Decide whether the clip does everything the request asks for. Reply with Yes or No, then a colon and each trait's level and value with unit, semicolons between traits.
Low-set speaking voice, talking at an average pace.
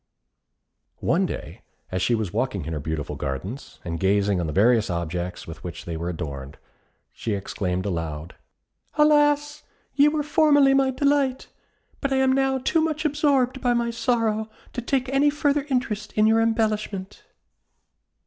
No: high, 220 Hz; average, 160 wpm